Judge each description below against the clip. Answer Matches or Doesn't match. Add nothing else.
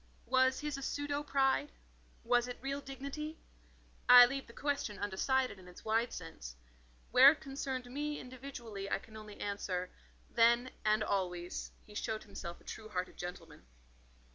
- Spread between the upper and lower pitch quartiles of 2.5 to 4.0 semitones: Doesn't match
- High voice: Matches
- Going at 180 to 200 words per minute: Doesn't match